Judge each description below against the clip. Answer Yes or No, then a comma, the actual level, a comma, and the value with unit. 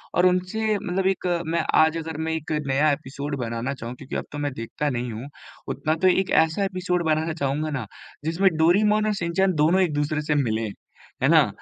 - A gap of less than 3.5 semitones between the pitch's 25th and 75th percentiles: No, average, 4.3 semitones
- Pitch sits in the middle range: Yes, medium, 160 Hz